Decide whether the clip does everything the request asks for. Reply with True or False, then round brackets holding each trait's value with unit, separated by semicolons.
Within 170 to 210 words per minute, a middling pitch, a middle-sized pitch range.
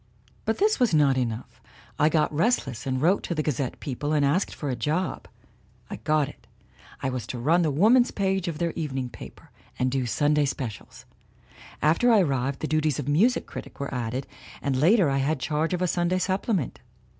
True (200 wpm; 150 Hz; 4.9 semitones)